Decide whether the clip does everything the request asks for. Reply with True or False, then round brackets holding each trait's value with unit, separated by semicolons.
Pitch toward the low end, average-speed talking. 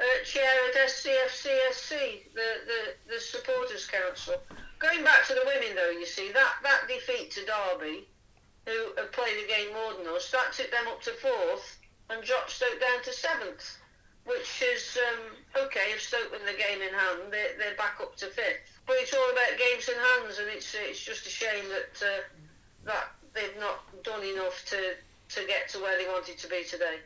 False (245 Hz; 195 wpm)